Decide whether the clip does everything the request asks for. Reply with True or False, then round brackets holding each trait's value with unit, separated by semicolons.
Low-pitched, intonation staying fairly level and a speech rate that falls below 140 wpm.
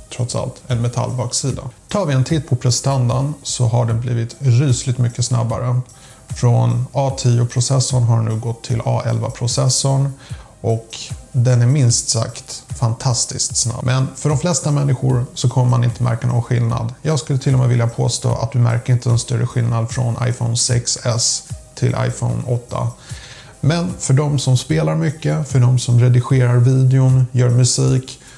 False (125 Hz; 1.7 semitones; 165 wpm)